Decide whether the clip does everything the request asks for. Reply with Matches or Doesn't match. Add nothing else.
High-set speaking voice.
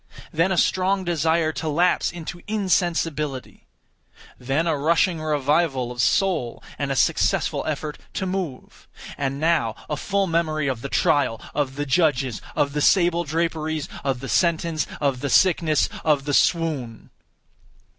Doesn't match